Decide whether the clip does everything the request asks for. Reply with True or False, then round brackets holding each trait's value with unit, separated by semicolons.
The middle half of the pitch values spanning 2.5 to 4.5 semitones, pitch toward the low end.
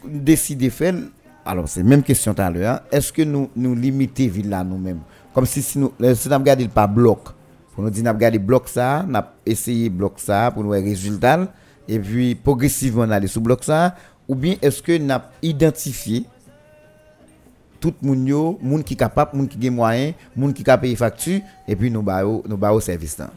False (5.0 semitones; 125 Hz)